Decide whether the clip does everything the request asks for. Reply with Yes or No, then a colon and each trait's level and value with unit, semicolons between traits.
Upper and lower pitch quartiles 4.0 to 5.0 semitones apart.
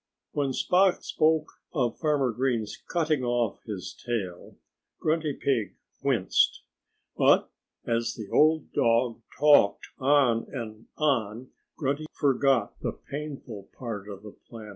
Yes: average, 4.7 semitones